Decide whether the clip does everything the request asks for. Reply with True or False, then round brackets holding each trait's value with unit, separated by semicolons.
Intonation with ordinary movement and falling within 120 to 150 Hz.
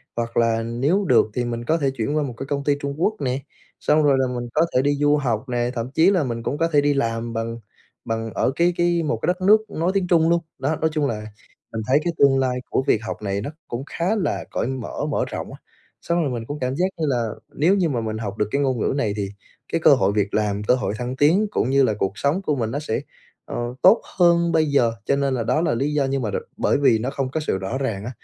True (5.0 semitones; 135 Hz)